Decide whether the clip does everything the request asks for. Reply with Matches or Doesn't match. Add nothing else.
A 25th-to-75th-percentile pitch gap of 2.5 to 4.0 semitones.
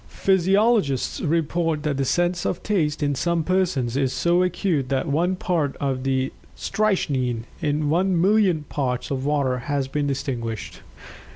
Doesn't match